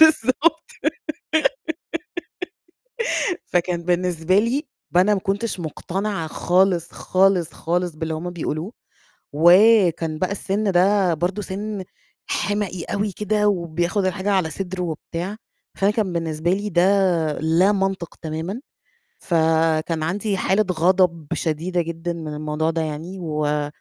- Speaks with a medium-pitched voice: Yes, medium, 180 Hz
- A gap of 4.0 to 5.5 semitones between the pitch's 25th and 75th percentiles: No, average, 3.3 semitones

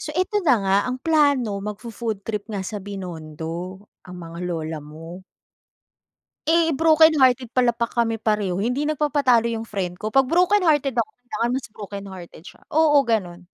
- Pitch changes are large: Yes, wide, 6.6 semitones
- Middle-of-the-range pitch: No, high, 225 Hz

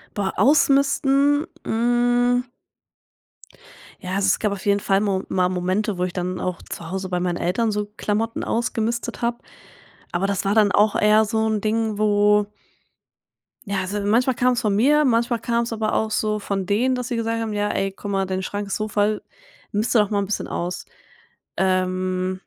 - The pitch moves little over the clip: No, average, 3.2 semitones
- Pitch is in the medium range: No, high, 210 Hz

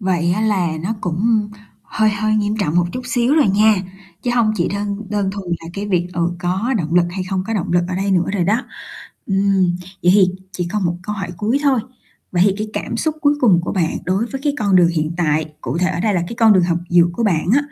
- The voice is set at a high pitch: Yes, high, 195 Hz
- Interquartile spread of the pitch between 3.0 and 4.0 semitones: Yes, average, 3.5 semitones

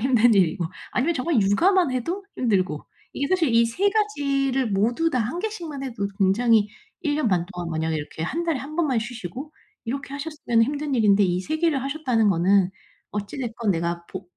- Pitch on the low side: No, high, 245 Hz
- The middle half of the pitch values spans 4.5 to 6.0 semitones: No, wide, 7.0 semitones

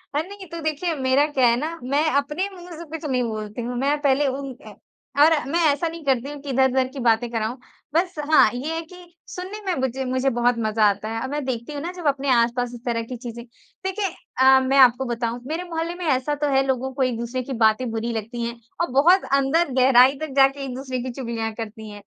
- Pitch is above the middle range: Yes, very high, 265 Hz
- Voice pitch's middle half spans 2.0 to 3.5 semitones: No, average, 4.1 semitones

